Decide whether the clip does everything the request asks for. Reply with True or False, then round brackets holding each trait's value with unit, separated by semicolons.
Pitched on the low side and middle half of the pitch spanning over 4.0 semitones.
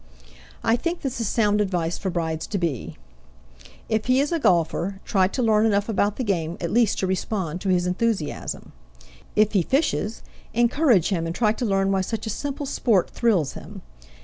False (205 Hz; 4.4 semitones)